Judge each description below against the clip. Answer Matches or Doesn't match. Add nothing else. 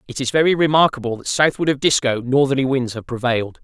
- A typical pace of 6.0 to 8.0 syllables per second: Matches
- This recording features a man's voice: Matches